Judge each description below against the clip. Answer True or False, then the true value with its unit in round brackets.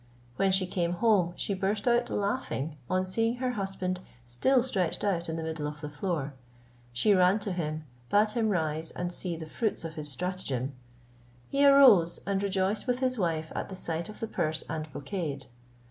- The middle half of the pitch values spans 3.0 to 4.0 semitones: False (4.6 semitones)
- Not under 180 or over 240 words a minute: True (190 wpm)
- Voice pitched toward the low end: False (185 Hz)